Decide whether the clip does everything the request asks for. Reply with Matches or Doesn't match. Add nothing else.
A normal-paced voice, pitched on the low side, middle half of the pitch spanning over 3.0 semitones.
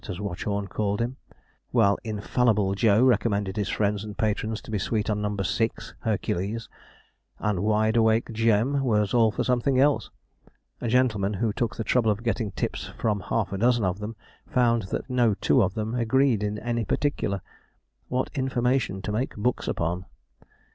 Doesn't match